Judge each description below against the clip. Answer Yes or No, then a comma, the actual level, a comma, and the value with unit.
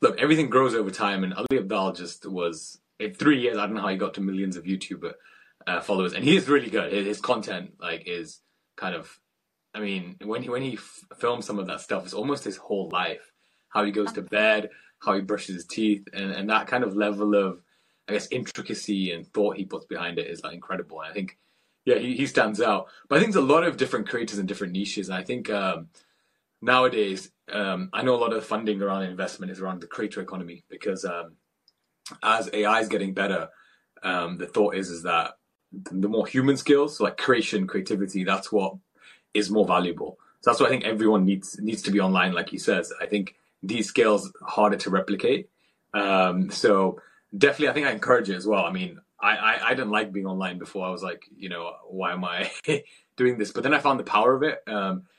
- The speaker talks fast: Yes, fast, 225 wpm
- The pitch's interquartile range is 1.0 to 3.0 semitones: Yes, narrow, 2.5 semitones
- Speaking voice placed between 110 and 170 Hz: No, low, 100 Hz